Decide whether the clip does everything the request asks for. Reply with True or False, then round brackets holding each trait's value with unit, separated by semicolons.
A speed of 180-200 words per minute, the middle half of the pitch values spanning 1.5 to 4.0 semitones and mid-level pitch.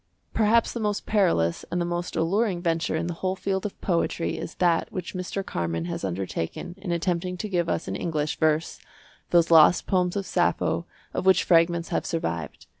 True (190 wpm; 2.6 semitones; 175 Hz)